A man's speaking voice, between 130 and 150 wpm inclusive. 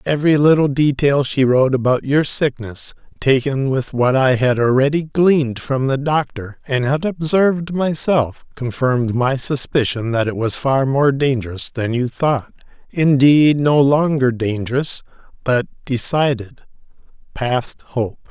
Yes: male; average, 140 wpm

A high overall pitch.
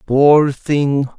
No: medium, 140 Hz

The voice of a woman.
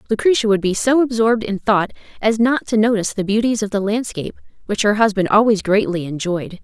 Yes: female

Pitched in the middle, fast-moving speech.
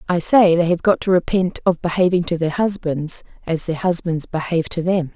Yes: medium, 170 Hz; fast, 210 wpm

